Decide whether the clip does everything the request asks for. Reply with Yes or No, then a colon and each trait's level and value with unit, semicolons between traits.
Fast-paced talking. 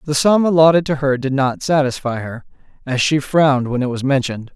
Yes: fast, 210 wpm